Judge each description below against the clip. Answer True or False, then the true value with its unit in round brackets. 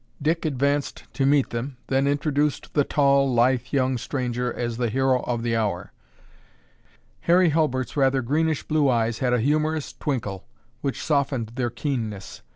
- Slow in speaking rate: False (155 wpm)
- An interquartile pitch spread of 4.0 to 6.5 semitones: False (3.2 semitones)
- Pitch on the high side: False (135 Hz)